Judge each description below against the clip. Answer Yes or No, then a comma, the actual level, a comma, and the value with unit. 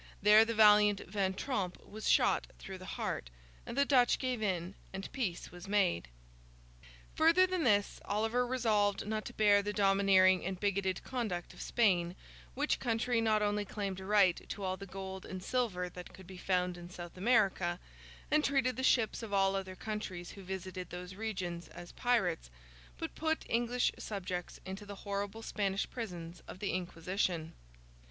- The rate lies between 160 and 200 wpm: Yes, average, 170 wpm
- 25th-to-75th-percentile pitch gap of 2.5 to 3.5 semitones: Yes, average, 3.1 semitones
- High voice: Yes, high, 200 Hz